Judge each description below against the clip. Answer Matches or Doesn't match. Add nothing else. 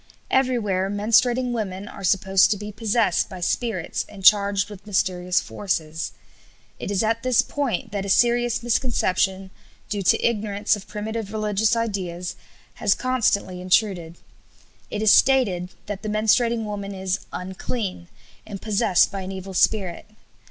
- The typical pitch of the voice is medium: Doesn't match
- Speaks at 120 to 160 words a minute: Matches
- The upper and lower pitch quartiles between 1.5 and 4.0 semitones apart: Matches